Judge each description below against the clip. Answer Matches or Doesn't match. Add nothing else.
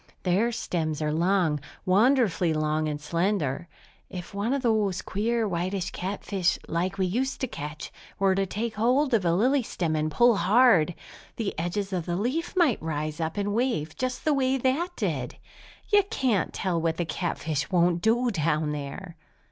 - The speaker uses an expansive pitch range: Matches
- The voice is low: Doesn't match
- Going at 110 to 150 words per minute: Doesn't match